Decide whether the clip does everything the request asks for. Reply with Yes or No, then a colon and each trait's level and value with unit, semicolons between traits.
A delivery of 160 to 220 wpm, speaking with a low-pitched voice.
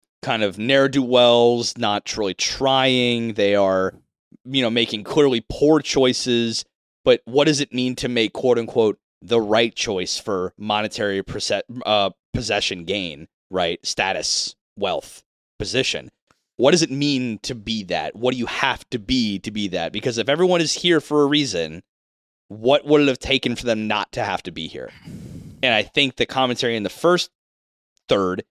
Yes: average, 180 wpm; low, 120 Hz